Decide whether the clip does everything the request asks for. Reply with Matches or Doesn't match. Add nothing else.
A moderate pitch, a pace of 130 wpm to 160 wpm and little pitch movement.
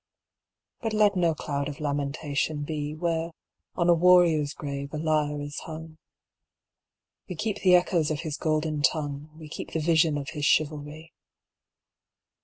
Matches